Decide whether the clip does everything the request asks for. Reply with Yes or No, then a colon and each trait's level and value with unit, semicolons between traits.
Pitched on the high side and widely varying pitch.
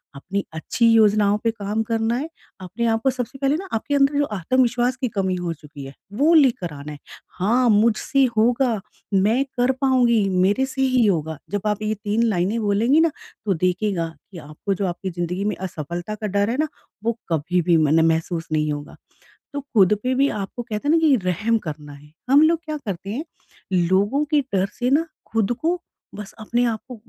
Yes: high, 210 Hz; wide, 5.8 semitones